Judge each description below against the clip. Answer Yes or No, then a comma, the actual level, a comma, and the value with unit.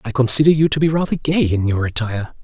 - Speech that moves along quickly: Yes, fast, 245 wpm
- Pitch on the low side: Yes, low, 130 Hz